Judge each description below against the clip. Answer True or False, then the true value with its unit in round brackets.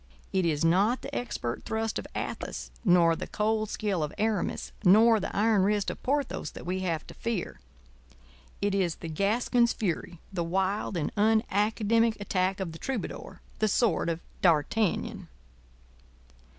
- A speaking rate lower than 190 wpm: True (140 wpm)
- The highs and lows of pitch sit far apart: False (4.7 semitones)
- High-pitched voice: True (195 Hz)